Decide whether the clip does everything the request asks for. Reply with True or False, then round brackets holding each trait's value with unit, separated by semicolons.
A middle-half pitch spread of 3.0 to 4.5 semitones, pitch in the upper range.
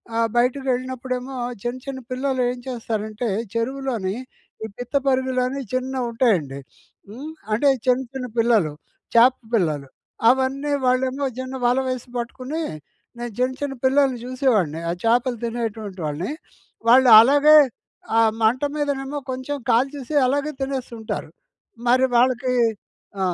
False (2.4 semitones; 255 Hz)